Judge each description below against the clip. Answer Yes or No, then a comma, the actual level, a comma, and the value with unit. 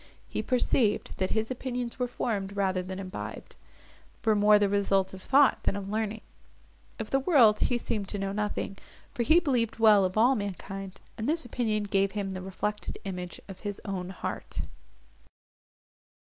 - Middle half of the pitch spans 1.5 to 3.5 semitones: Yes, average, 3.1 semitones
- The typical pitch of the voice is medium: No, high, 210 Hz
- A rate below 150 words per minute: No, average, 170 wpm